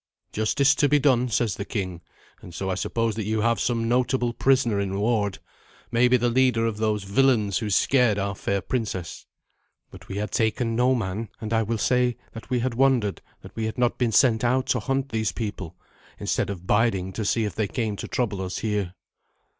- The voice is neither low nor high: No, low, 115 Hz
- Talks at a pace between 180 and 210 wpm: Yes, fast, 205 wpm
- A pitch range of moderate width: Yes, average, 3.5 semitones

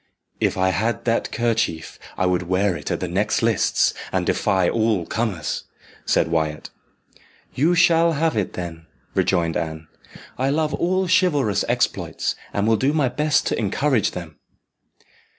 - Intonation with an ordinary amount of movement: No, wide, 8.6 semitones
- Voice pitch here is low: Yes, low, 110 Hz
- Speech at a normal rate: Yes, average, 150 wpm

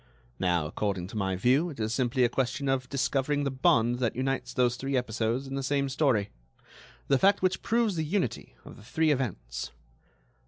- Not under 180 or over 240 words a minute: Yes, average, 185 wpm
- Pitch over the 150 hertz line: No, low, 130 Hz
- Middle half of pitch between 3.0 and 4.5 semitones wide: Yes, average, 4.0 semitones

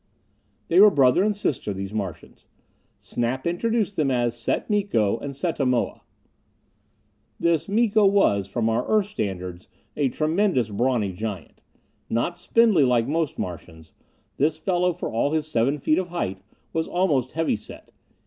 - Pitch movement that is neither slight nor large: No, wide, 7.7 semitones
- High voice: No, medium, 140 Hz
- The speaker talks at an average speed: Yes, average, 150 wpm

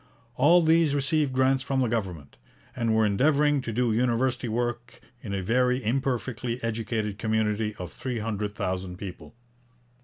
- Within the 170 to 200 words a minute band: No, average, 150 wpm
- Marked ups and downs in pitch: No, average, 3.7 semitones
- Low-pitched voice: Yes, low, 115 Hz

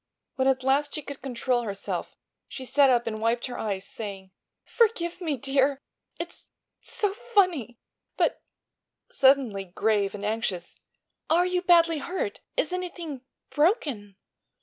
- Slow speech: Yes, slow, 130 wpm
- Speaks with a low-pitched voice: No, very high, 270 Hz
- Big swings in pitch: Yes, wide, 7.4 semitones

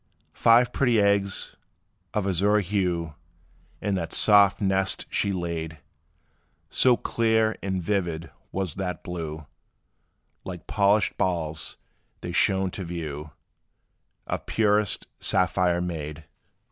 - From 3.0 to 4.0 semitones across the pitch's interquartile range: Yes, average, 3.3 semitones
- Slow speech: Yes, slow, 110 wpm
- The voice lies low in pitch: Yes, very low, 95 Hz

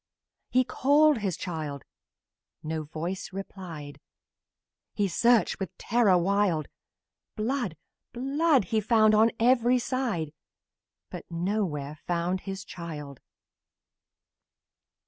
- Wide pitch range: Yes, wide, 6.2 semitones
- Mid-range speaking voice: No, high, 195 Hz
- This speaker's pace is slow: Yes, slow, 95 wpm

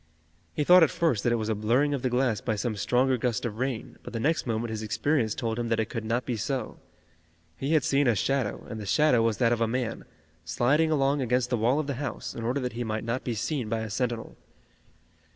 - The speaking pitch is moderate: No, low, 120 Hz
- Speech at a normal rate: No, fast, 250 wpm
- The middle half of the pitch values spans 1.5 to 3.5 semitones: Yes, average, 3.2 semitones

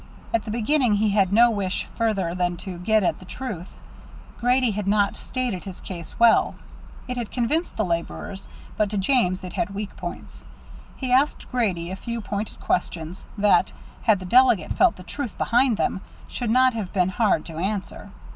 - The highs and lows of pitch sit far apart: No, average, 4.4 semitones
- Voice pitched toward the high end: Yes, high, 210 Hz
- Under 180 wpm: No, average, 185 wpm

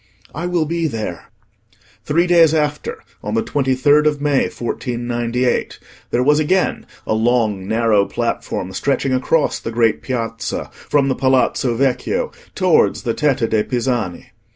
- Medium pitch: No, low, 130 Hz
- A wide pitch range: No, average, 4.4 semitones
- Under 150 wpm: Yes, average, 140 wpm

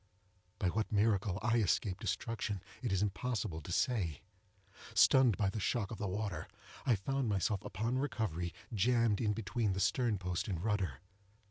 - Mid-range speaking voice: No, low, 105 Hz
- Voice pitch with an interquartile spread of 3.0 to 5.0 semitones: Yes, average, 3.5 semitones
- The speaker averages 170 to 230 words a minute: No, average, 160 wpm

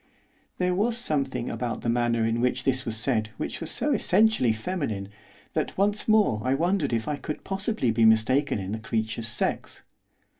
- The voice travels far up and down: Yes, wide, 8.4 semitones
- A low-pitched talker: Yes, low, 130 Hz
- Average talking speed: Yes, average, 180 wpm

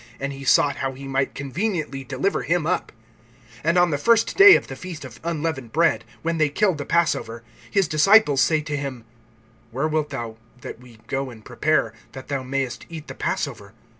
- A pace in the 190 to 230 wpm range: Yes, average, 195 wpm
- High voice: No, medium, 145 Hz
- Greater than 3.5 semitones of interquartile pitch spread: Yes, average, 3.9 semitones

